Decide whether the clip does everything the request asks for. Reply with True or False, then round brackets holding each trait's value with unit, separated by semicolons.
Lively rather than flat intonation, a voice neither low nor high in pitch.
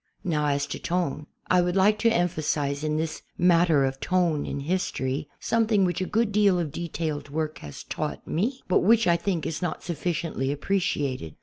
False (3.9 semitones; 170 Hz)